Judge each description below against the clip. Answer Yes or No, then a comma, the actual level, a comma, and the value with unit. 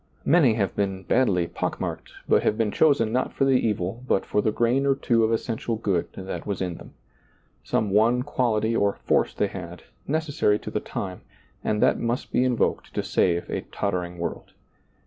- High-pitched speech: No, low, 110 Hz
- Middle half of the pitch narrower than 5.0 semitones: Yes, average, 4.3 semitones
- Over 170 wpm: Yes, average, 190 wpm